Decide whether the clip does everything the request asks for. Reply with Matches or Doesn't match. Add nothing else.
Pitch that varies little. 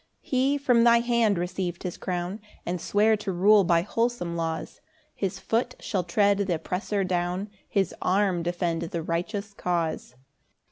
Doesn't match